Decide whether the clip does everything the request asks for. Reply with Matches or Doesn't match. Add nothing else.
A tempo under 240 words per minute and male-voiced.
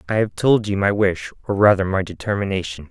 Matches